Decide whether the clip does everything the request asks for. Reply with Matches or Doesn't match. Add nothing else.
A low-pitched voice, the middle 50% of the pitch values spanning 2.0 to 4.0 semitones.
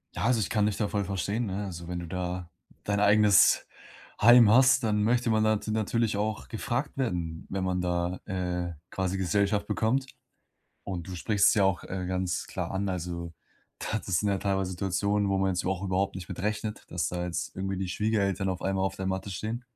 Matches